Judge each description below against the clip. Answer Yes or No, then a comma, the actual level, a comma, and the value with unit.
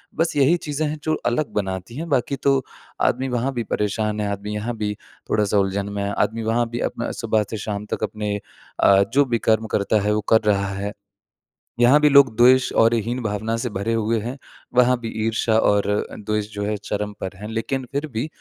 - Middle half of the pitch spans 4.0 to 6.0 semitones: No, average, 3.2 semitones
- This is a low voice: Yes, low, 110 Hz